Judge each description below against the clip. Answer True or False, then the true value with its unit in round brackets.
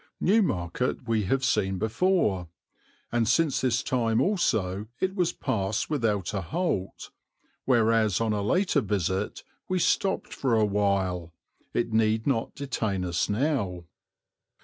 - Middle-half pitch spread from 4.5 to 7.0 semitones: True (5.3 semitones)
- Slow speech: True (130 wpm)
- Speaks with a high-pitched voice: False (110 Hz)